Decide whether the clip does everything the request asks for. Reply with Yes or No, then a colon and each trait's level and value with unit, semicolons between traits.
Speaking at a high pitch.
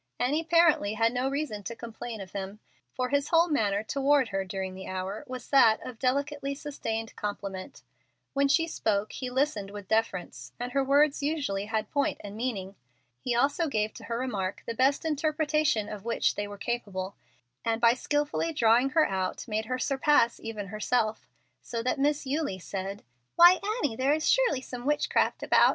Yes: high, 240 Hz